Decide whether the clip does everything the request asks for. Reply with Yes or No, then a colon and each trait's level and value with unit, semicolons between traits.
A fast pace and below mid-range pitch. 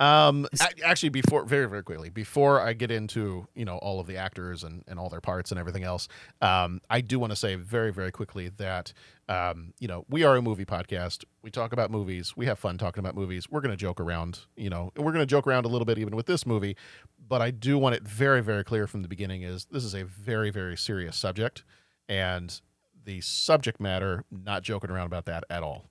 Yes: fast, 235 wpm; low, 100 Hz